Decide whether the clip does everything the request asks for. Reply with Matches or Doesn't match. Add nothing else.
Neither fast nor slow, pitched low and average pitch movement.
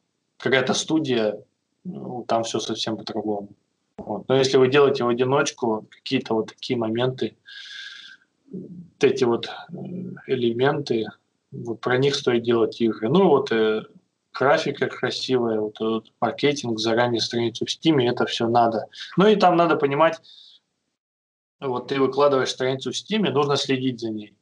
Doesn't match